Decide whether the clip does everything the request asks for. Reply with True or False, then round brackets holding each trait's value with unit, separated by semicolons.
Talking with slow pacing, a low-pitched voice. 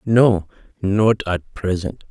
True (115 wpm; 100 Hz)